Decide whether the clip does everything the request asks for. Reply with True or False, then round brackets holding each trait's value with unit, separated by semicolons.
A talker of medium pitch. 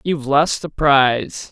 True (145 Hz)